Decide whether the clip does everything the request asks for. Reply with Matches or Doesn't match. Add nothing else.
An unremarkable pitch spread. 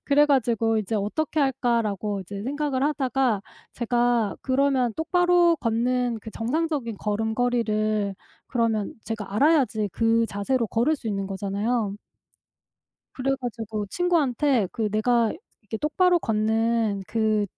Matches